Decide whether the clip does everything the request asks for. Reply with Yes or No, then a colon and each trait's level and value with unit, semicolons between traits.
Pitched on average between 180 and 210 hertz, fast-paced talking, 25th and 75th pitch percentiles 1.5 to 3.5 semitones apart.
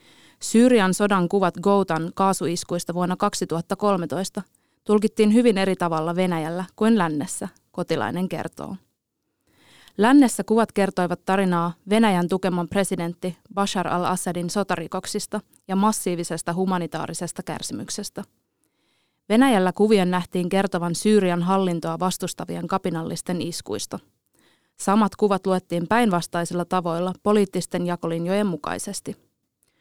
No: medium, 185 Hz; slow, 95 wpm; narrow, 2.6 semitones